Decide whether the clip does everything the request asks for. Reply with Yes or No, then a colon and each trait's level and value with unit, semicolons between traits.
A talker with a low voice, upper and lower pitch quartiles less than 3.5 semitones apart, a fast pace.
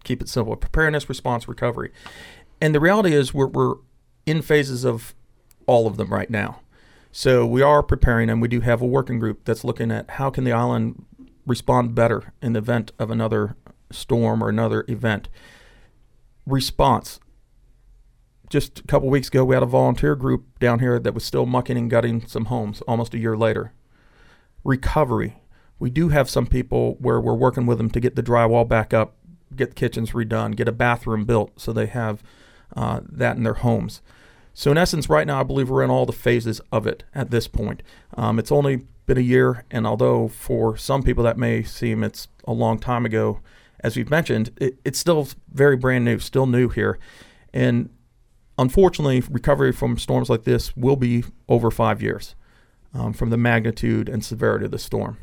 No: low, 120 Hz; narrow, 2.4 semitones; average, 190 wpm